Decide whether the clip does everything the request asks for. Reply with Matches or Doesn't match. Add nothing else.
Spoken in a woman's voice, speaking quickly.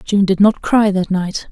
Matches